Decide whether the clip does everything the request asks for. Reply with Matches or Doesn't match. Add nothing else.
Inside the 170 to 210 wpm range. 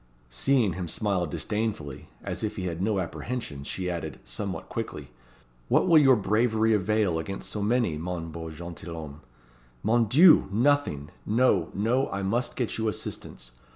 Doesn't match